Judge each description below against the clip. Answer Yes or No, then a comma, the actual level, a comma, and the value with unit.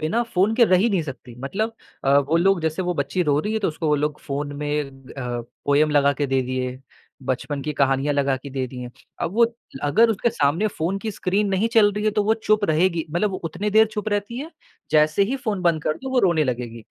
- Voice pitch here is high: No, medium, 165 Hz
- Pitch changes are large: Yes, wide, 6.7 semitones